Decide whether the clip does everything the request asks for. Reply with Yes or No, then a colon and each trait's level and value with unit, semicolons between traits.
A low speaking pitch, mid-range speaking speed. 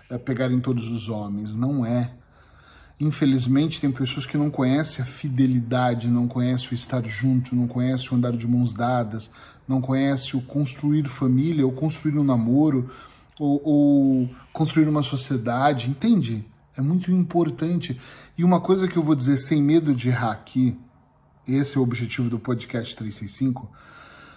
Yes: low, 130 Hz; average, 160 wpm